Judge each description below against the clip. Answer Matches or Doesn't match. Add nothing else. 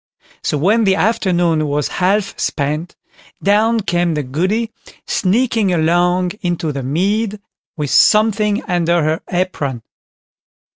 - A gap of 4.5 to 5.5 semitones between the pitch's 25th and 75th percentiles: Matches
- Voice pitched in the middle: Matches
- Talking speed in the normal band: Doesn't match